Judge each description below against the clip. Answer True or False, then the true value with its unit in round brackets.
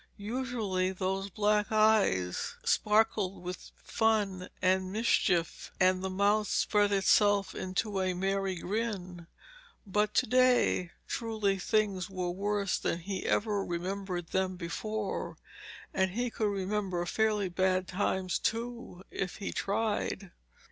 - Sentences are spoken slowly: True (120 wpm)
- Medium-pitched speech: False (195 Hz)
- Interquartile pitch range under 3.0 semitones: True (2.4 semitones)